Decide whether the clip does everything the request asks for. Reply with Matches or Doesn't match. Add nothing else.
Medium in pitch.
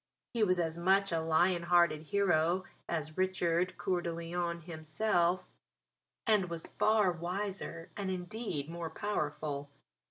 Matches